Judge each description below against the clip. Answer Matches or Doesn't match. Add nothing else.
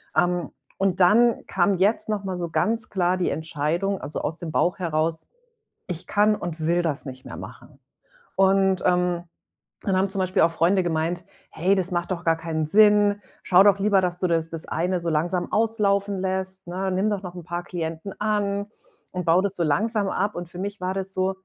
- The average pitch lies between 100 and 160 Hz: Doesn't match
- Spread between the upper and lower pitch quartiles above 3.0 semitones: Doesn't match